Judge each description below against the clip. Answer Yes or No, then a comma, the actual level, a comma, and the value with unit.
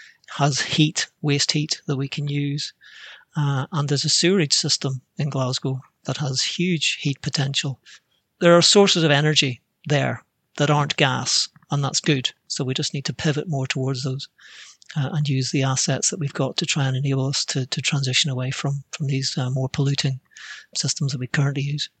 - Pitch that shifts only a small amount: Yes, narrow, 2.2 semitones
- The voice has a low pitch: No, medium, 145 Hz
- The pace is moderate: Yes, average, 190 wpm